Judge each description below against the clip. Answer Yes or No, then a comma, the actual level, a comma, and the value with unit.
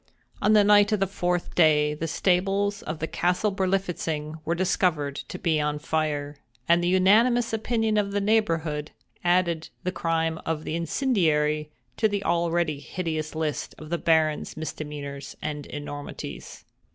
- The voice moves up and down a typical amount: Yes, average, 4.1 semitones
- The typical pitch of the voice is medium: Yes, medium, 165 Hz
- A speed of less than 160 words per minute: Yes, average, 150 wpm